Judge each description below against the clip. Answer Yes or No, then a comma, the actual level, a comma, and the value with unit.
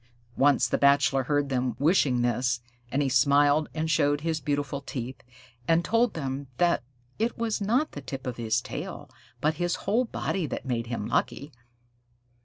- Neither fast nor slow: Yes, average, 170 wpm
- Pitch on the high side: No, medium, 145 Hz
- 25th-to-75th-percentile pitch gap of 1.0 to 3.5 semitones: No, average, 4.0 semitones